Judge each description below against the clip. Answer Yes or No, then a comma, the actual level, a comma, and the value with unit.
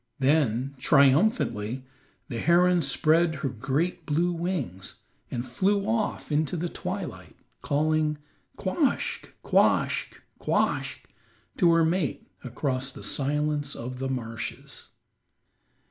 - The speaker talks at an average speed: No, slow, 105 wpm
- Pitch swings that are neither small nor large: Yes, average, 4.7 semitones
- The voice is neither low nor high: Yes, medium, 150 Hz